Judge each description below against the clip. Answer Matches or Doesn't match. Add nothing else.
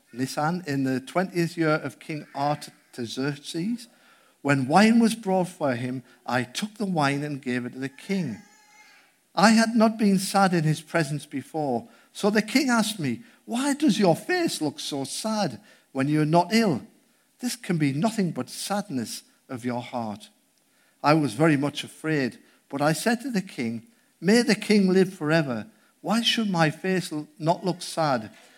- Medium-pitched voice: Matches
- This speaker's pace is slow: Doesn't match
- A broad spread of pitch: Matches